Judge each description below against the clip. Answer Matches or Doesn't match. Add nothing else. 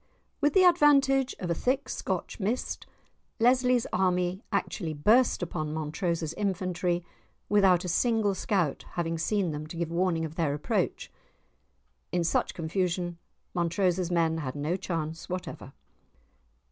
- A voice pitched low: Doesn't match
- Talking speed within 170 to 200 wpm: Doesn't match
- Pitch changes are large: Doesn't match